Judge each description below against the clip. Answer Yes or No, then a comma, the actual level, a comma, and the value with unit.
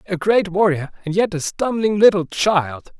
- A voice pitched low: No, medium, 185 Hz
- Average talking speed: Yes, average, 180 wpm